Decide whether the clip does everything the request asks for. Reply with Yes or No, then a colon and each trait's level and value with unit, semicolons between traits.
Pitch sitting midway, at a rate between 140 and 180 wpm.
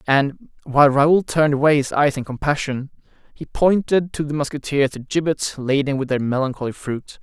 Yes: medium, 145 Hz; average, 175 wpm